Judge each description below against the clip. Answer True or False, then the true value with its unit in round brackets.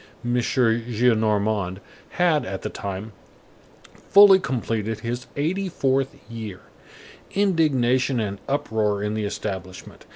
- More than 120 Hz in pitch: False (115 Hz)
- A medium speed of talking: False (105 wpm)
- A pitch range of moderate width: True (4.6 semitones)